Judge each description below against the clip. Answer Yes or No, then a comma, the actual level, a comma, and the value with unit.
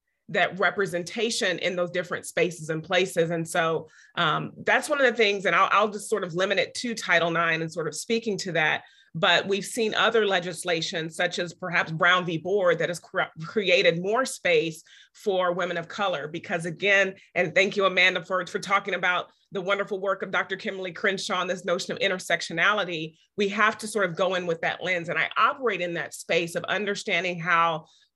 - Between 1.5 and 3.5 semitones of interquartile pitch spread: Yes, average, 2.9 semitones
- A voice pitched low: No, medium, 185 Hz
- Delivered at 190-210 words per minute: Yes, average, 200 wpm